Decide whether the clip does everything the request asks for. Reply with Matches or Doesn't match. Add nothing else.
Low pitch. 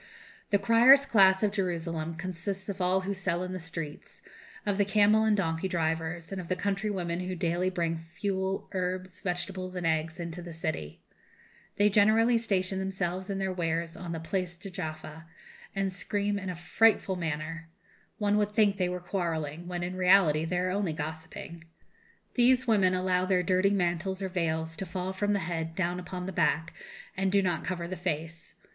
Doesn't match